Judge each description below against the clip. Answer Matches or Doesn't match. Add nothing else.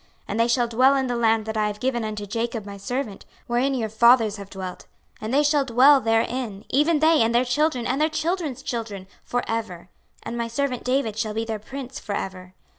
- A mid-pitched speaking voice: Doesn't match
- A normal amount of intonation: Matches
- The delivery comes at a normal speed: Doesn't match